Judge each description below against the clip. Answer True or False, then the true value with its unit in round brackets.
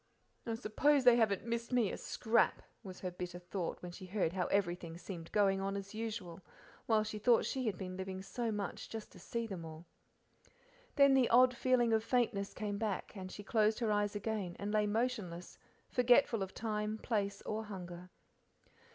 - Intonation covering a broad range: False (3.4 semitones)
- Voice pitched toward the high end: True (210 Hz)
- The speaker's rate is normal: True (185 wpm)